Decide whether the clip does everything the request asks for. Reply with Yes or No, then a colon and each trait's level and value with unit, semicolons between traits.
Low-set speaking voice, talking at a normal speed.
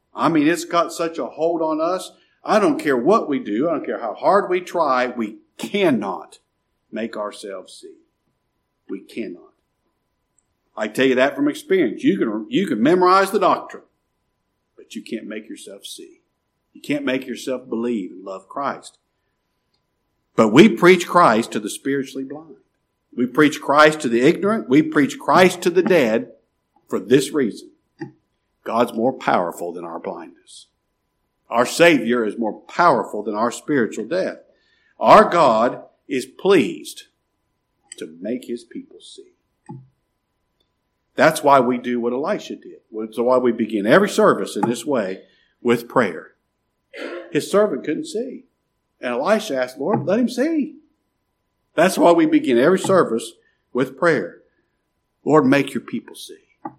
No: medium, 175 Hz; average, 155 wpm